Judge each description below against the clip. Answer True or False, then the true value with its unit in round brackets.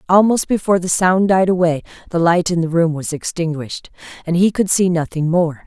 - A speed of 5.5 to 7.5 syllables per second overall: True (5.6 syllables/s)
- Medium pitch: True (175 Hz)